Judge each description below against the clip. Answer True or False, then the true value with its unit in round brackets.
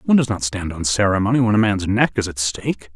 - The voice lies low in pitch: True (100 Hz)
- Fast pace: True (265 wpm)